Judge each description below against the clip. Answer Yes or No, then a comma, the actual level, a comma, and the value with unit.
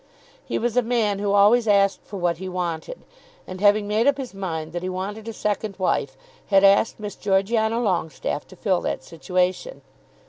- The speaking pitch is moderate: No, high, 200 Hz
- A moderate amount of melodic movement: Yes, average, 3.0 semitones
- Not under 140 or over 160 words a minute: No, average, 185 wpm